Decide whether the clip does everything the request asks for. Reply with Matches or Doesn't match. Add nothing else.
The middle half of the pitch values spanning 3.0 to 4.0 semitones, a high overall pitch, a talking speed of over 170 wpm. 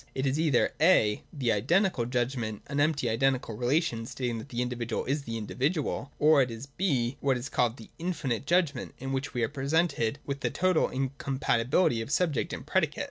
Doesn't match